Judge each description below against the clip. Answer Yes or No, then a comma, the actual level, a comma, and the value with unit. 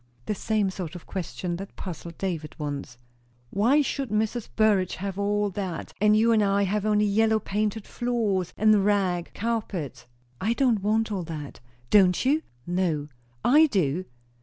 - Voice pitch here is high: Yes, high, 200 Hz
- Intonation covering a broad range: No, average, 3.3 semitones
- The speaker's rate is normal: Yes, average, 160 wpm